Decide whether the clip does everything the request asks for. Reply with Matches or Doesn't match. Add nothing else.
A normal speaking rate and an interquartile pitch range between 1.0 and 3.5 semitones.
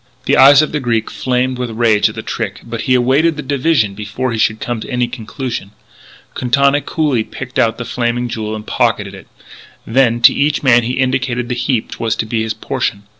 Doesn't match